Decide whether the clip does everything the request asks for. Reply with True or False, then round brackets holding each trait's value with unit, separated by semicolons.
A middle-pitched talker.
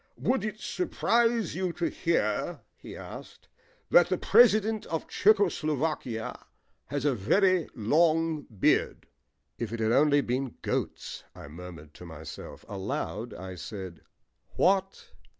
True (150 Hz)